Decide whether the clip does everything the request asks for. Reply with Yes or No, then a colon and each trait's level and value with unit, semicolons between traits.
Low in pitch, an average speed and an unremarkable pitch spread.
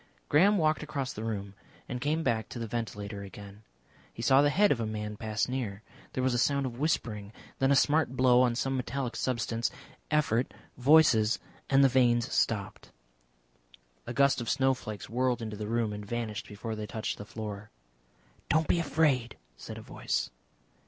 Yes: low, 120 Hz; average, 180 wpm; average, 4.0 semitones